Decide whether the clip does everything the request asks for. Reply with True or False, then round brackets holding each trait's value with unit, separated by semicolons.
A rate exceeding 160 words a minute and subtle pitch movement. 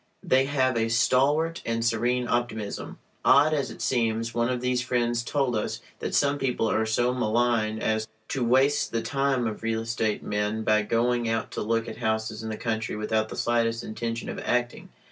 True (190 wpm; 2.2 semitones)